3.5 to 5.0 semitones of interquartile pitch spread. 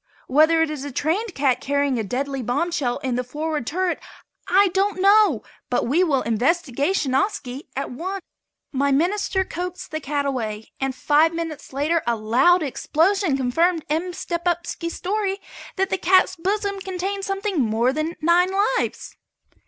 No: wide, 5.4 semitones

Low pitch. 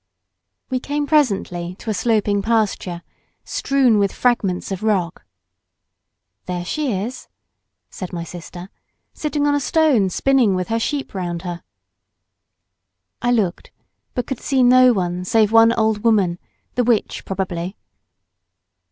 No: high, 215 Hz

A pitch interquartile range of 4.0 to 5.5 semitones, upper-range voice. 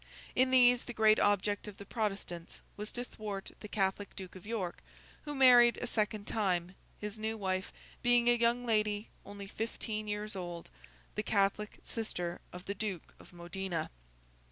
No: average, 2.8 semitones; high, 210 Hz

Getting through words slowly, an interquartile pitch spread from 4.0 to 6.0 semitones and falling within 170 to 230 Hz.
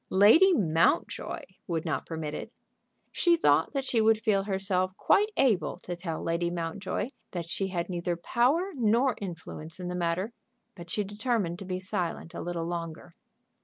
No: average, 165 wpm; average, 4.3 semitones; medium, 185 Hz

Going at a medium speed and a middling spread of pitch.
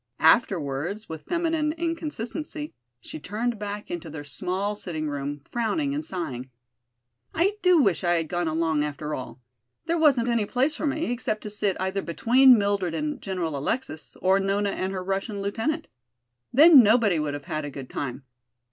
No: average, 170 wpm; wide, 8.3 semitones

